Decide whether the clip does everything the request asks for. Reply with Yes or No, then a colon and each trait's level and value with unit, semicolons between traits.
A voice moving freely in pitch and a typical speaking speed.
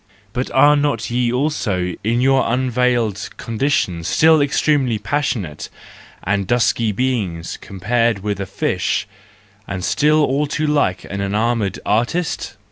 No: wide, 5.8 semitones; slow, 125 wpm